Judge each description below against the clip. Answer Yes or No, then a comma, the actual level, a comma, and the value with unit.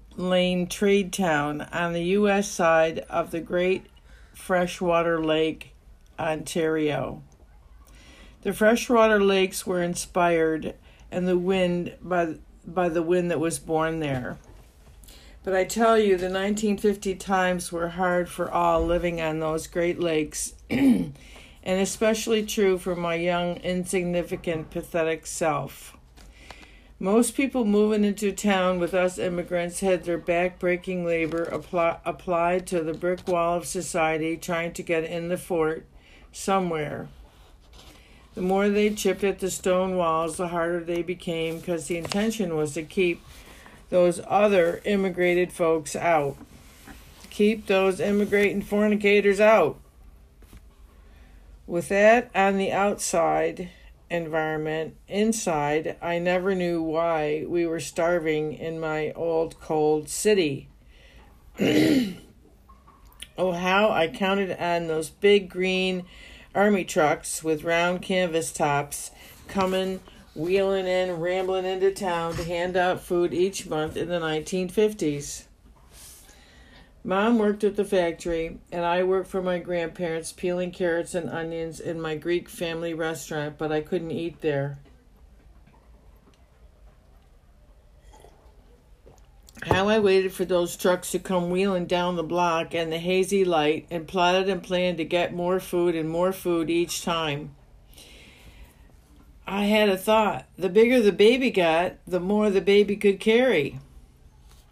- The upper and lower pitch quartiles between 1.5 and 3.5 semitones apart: Yes, average, 3.0 semitones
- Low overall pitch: No, medium, 175 Hz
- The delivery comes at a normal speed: No, slow, 130 wpm